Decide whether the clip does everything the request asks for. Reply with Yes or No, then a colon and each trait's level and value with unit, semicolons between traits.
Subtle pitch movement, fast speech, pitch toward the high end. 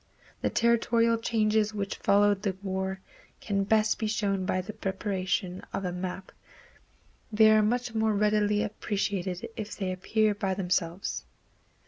No: narrow, 2.2 semitones; average, 140 wpm; high, 205 Hz